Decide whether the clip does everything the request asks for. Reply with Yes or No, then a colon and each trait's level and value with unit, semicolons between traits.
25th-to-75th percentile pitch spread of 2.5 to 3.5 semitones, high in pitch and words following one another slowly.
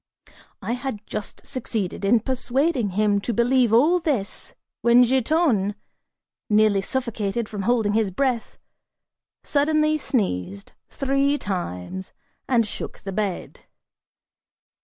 No: average, 4.6 semitones; high, 230 Hz; slow, 110 wpm